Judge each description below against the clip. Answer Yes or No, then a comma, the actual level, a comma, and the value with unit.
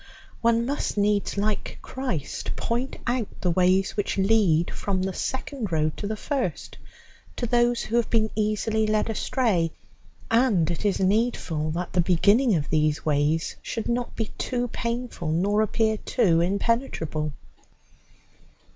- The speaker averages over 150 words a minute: No, average, 145 wpm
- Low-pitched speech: No, high, 210 Hz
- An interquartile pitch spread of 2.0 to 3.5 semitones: No, average, 5.1 semitones